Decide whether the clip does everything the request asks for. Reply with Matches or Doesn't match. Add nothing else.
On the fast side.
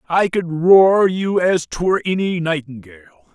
Doesn't match